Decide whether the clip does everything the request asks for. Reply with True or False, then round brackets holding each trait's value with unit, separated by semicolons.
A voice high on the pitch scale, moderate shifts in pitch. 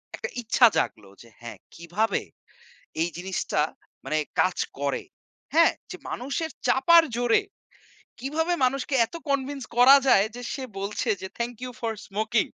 False (240 Hz; 6.2 semitones)